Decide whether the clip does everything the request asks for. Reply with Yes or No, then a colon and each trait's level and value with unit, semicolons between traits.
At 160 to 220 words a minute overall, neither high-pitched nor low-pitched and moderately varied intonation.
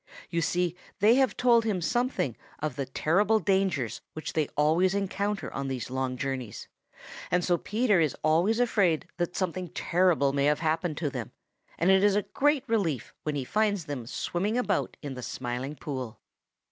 No: average, 175 wpm; medium, 170 Hz; wide, 6.2 semitones